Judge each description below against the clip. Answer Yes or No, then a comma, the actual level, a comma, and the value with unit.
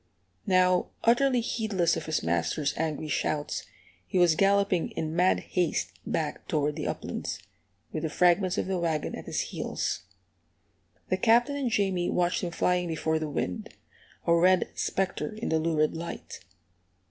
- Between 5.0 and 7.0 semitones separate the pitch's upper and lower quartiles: No, average, 3.4 semitones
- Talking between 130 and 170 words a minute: Yes, average, 155 wpm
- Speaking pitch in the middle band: Yes, medium, 175 Hz